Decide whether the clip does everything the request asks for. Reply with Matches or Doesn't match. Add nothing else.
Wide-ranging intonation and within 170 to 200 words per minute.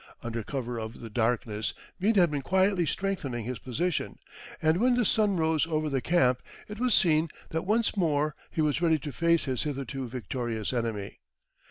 Matches